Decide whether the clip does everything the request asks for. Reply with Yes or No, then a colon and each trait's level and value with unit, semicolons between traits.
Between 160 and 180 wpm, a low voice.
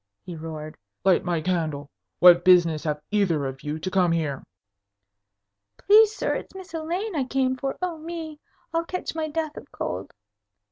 No: average, 170 wpm; medium, 185 Hz